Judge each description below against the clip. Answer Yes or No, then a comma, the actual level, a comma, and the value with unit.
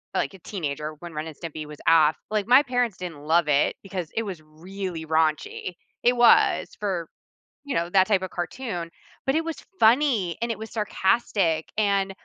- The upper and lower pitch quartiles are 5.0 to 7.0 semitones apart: Yes, wide, 5.4 semitones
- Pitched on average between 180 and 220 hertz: Yes, medium, 185 Hz